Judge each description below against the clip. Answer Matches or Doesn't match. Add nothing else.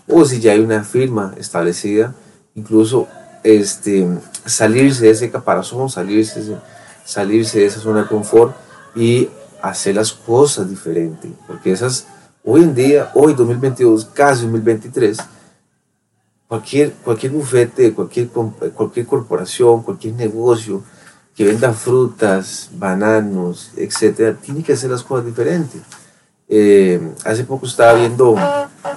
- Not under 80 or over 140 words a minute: Matches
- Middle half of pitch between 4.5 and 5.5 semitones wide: Doesn't match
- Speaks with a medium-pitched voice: Doesn't match